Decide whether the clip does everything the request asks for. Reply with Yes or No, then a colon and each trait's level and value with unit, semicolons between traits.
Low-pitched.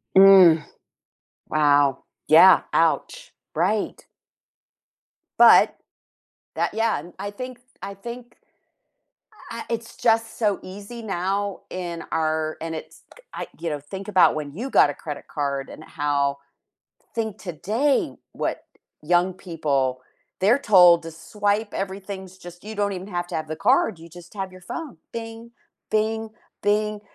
No: high, 190 Hz